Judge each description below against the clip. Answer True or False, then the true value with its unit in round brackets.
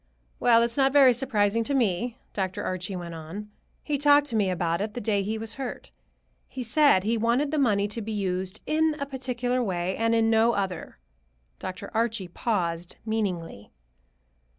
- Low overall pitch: False (220 Hz)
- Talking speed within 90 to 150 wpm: False (175 wpm)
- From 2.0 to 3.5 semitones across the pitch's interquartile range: False (4.7 semitones)